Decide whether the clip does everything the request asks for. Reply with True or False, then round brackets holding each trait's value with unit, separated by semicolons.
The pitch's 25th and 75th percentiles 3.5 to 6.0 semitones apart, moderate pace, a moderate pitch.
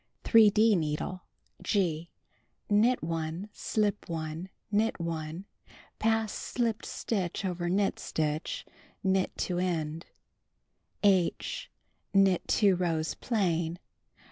False (3.9 semitones; 100 wpm; 180 Hz)